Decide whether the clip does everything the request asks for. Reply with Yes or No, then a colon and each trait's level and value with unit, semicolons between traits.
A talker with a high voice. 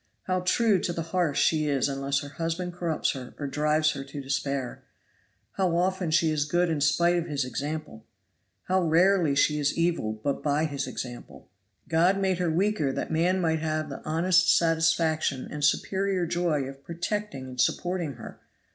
No: medium, 160 Hz